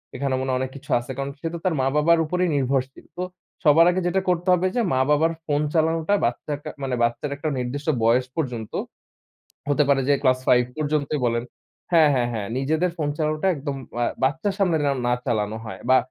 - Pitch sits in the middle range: Yes, medium, 145 Hz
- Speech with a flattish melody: No, average, 3.8 semitones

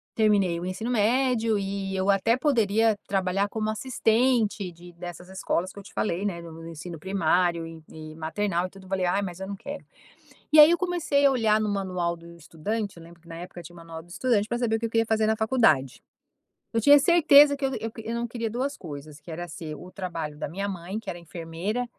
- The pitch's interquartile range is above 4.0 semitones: Yes, average, 4.9 semitones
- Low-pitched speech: No, high, 195 Hz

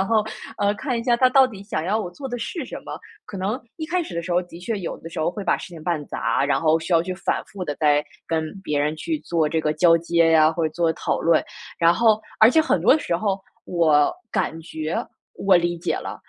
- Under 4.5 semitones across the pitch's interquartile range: No, average, 5.1 semitones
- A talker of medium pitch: Yes, medium, 175 Hz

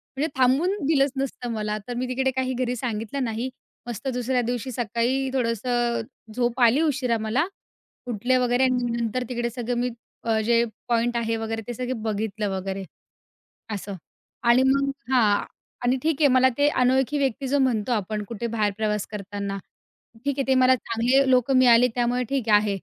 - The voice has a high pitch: Yes, high, 245 Hz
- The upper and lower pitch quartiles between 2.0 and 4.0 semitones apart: Yes, narrow, 2.6 semitones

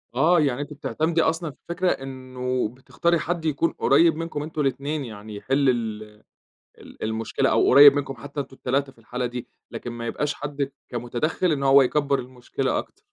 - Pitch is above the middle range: No, medium, 140 Hz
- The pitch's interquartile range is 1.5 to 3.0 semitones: No, average, 3.5 semitones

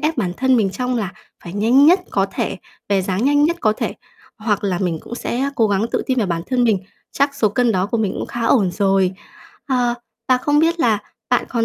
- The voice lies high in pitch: Yes, high, 230 Hz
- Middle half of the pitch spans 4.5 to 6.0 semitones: Yes, average, 4.9 semitones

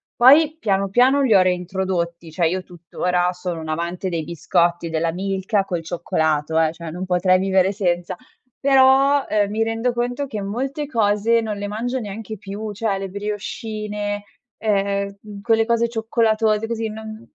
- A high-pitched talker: Yes, high, 200 Hz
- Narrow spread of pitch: No, average, 3.9 semitones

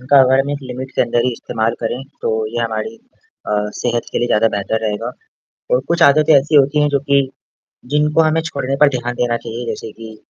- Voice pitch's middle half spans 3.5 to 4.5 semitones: Yes, average, 3.8 semitones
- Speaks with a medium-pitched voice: No, low, 125 Hz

